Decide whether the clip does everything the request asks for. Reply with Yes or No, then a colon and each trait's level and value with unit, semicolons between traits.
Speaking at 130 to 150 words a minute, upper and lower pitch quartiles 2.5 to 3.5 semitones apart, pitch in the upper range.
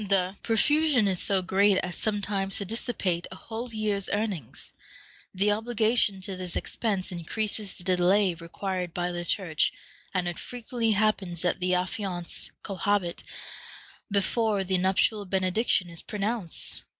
Yes: average, 140 wpm; average, 2.9 semitones; high, 195 Hz